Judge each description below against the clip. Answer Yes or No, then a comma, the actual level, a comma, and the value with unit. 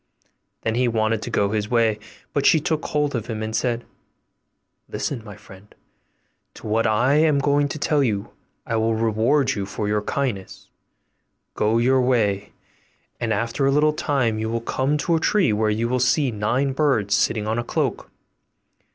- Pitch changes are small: No, average, 4.4 semitones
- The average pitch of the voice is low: Yes, low, 115 Hz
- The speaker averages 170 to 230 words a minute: Yes, average, 180 wpm